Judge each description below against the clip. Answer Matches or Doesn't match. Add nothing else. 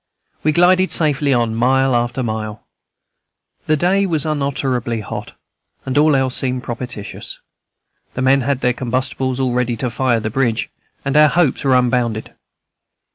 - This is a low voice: Matches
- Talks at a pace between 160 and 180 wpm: Doesn't match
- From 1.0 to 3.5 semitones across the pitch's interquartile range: Matches